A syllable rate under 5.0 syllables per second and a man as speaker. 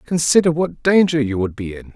No: 5.4 syllables/s; male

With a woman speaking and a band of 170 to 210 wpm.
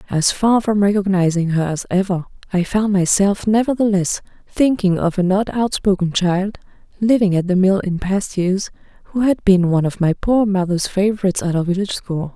Yes: female; average, 180 wpm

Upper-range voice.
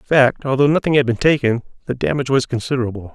No: low, 130 Hz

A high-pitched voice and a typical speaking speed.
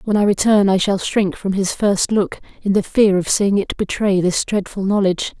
No: high, 200 Hz; fast, 220 wpm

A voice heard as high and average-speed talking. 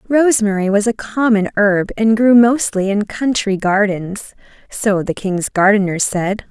Yes: high, 210 Hz; average, 150 wpm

